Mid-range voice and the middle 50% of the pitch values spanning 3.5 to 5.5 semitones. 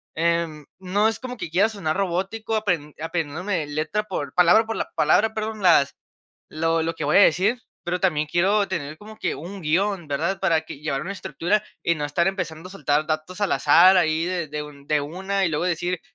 Yes: medium, 175 Hz; average, 4.1 semitones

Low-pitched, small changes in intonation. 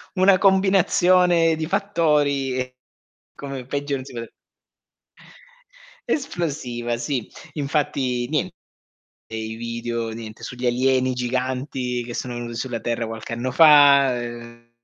No: low, 130 Hz; average, 4.0 semitones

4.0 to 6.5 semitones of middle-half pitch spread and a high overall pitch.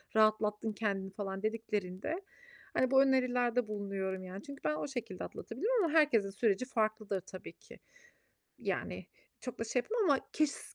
Yes: average, 5.0 semitones; high, 220 Hz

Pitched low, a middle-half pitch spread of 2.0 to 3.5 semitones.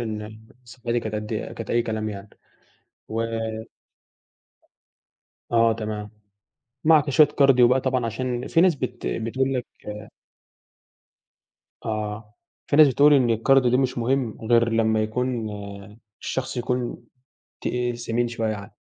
Yes: low, 120 Hz; narrow, 2.6 semitones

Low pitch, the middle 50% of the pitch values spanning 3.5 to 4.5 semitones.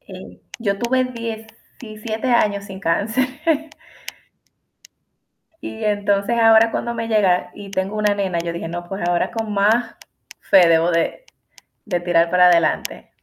No: high, 205 Hz; average, 4.0 semitones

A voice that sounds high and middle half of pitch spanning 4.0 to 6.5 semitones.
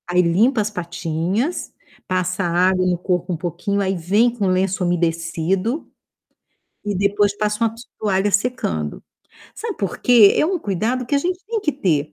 Yes: high, 195 Hz; average, 4.3 semitones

